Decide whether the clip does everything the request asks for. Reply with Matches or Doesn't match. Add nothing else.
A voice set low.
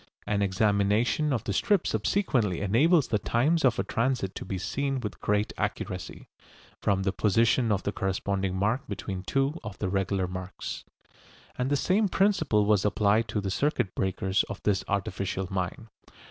Matches